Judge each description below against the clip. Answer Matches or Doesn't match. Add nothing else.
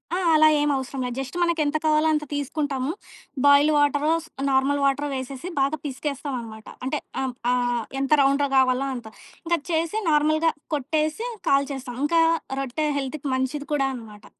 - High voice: Matches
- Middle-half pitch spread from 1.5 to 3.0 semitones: Matches